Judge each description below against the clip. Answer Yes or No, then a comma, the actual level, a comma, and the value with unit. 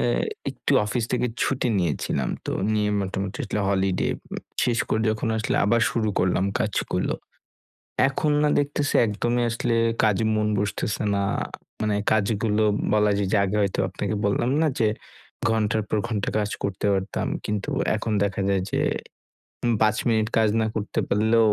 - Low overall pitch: Yes, low, 105 Hz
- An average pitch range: No, narrow, 2.1 semitones